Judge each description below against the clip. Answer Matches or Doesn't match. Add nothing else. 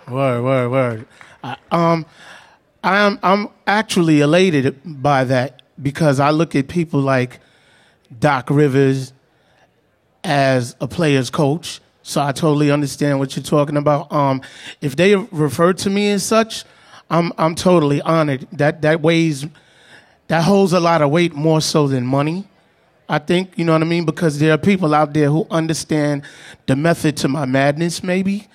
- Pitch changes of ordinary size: Matches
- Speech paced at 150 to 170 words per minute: Matches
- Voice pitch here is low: Doesn't match